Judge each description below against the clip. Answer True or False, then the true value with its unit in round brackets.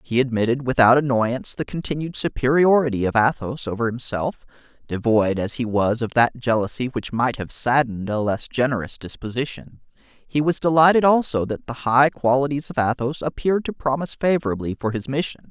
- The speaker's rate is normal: True (165 wpm)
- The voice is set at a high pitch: False (130 Hz)